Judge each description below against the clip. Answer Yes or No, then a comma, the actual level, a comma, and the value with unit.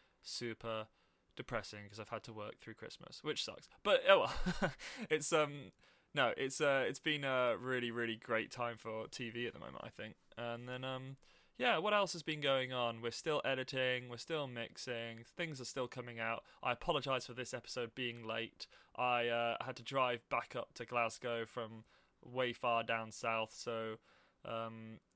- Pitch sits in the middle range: No, low, 120 Hz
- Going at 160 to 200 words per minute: Yes, average, 185 wpm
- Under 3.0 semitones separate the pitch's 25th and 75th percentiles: Yes, narrow, 2.4 semitones